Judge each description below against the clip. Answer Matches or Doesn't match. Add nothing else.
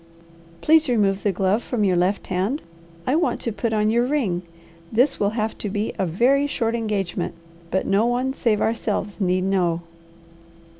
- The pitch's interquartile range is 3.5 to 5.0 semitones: Matches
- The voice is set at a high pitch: Matches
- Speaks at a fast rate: Doesn't match